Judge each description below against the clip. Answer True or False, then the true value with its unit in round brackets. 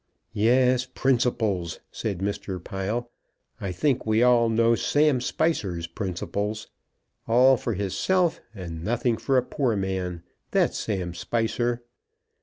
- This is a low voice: True (115 Hz)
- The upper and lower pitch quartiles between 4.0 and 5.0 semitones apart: True (4.4 semitones)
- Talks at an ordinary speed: False (120 wpm)